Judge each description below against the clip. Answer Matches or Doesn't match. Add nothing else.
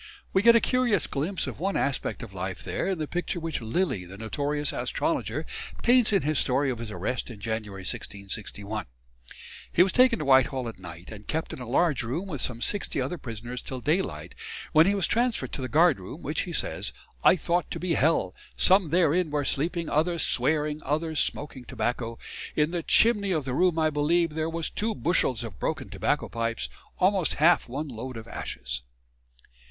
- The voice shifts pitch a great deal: Matches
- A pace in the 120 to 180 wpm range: Doesn't match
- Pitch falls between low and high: Matches